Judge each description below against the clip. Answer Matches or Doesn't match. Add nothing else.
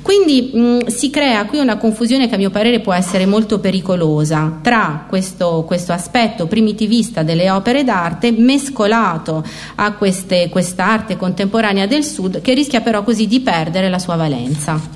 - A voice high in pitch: Matches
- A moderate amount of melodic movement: Matches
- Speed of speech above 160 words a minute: Doesn't match